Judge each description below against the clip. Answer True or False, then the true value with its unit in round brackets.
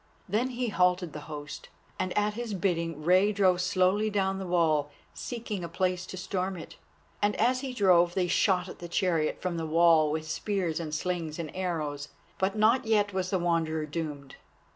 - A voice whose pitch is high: False (180 Hz)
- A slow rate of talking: False (185 wpm)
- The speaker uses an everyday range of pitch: True (3.4 semitones)